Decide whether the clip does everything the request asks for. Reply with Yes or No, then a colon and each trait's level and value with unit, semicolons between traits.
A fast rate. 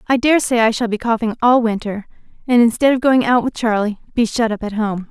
Yes: fast, 245 wpm